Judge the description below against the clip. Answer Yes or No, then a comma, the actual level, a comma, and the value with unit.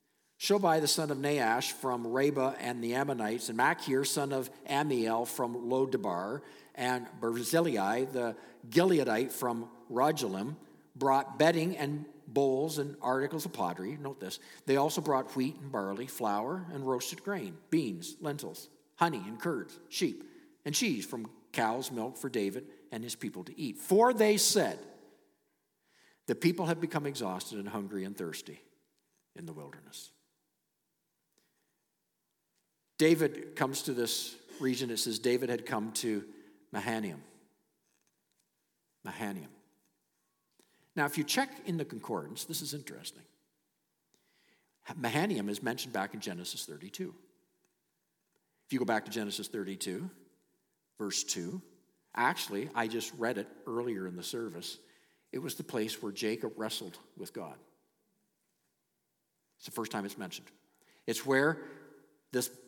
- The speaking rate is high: No, slow, 135 wpm